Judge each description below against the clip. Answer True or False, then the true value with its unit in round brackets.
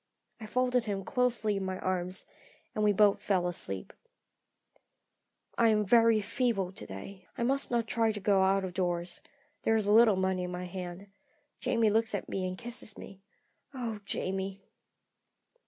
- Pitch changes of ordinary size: True (3.4 semitones)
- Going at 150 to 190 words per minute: True (165 wpm)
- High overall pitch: True (200 Hz)